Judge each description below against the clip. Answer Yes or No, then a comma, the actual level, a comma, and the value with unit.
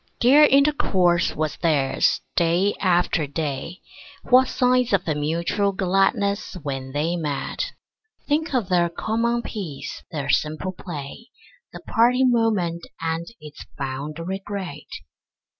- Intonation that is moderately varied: No, wide, 6.2 semitones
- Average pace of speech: No, slow, 115 wpm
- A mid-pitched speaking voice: Yes, medium, 175 Hz